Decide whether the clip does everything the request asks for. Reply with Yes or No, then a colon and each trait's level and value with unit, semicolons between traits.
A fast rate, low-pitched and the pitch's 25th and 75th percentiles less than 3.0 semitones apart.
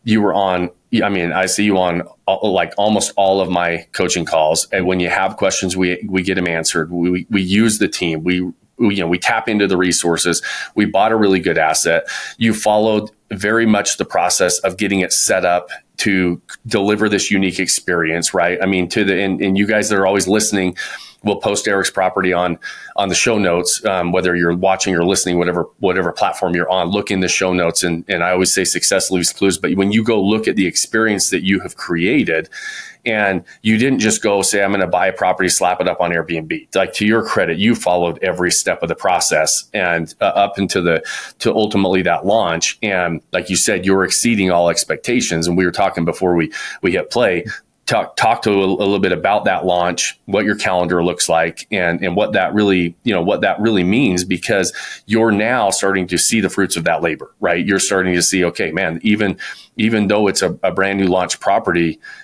Yes: fast, 225 wpm; very low, 95 Hz; narrow, 2.5 semitones